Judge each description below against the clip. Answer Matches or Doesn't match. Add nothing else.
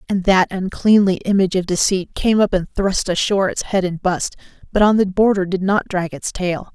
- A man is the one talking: Doesn't match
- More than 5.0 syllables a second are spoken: Matches